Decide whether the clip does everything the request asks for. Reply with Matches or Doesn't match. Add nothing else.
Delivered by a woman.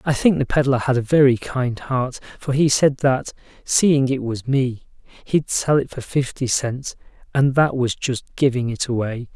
Doesn't match